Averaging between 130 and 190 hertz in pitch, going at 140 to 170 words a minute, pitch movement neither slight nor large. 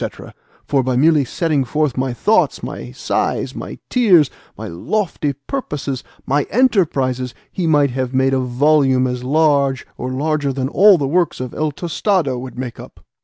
Yes: medium, 140 Hz; average, 165 wpm; average, 3.6 semitones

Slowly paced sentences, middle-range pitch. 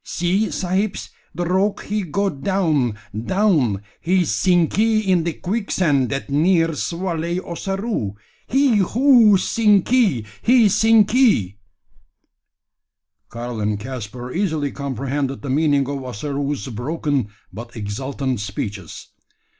Yes: slow, 105 wpm; medium, 165 Hz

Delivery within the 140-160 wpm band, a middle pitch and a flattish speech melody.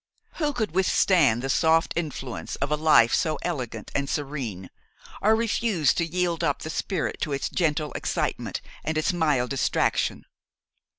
No: average, 155 wpm; medium, 155 Hz; average, 4.1 semitones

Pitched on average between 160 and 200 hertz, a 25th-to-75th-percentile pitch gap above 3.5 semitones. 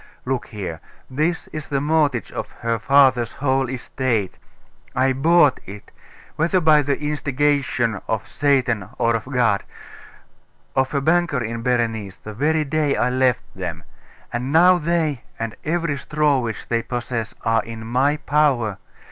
No: low, 130 Hz; average, 4.4 semitones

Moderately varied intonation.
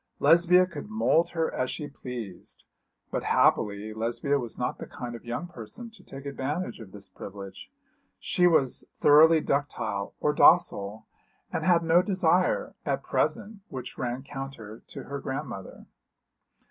No: wide, 6.6 semitones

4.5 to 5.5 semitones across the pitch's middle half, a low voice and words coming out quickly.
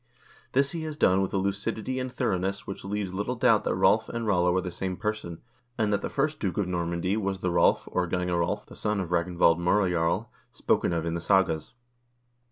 No: average, 3.2 semitones; very low, 95 Hz; fast, 210 wpm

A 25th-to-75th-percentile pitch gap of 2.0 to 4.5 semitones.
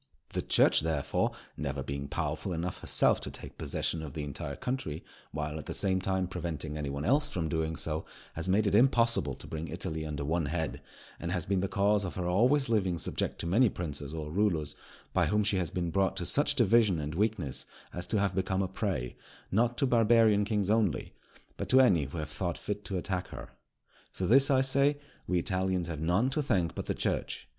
No: average, 5.1 semitones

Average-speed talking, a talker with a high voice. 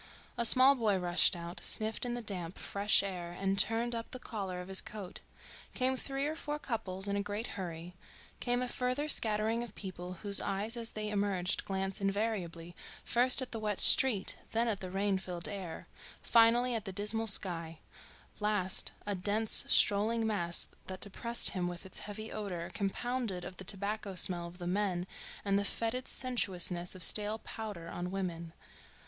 Yes: average, 180 wpm; high, 200 Hz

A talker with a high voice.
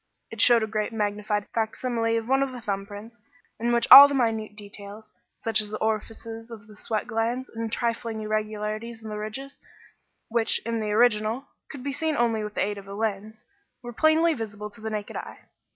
Yes: high, 220 Hz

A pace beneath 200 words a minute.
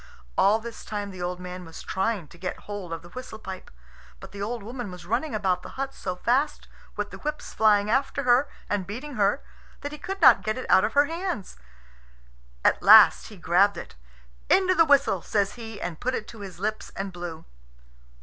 No: fast, 205 wpm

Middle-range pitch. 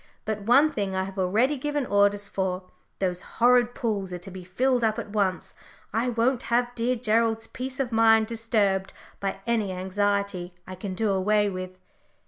No: high, 210 Hz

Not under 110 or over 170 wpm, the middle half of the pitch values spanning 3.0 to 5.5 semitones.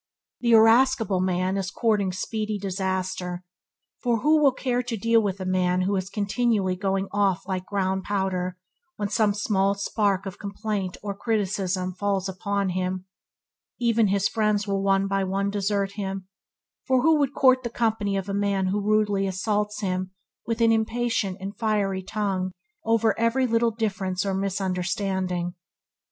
No: average, 155 wpm; narrow, 2.6 semitones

